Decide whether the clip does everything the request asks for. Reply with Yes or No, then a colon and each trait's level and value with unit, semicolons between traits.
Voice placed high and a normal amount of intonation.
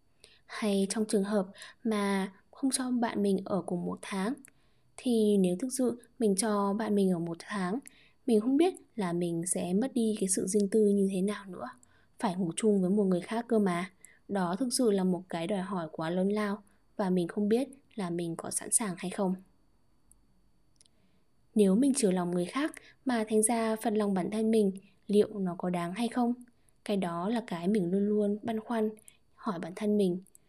Yes: high, 205 Hz; average, 3.4 semitones